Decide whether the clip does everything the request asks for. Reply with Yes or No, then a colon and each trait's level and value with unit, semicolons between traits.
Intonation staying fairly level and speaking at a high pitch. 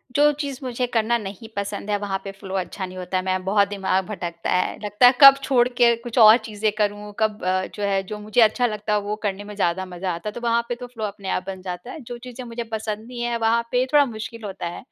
No: average, 3.5 semitones; high, 210 Hz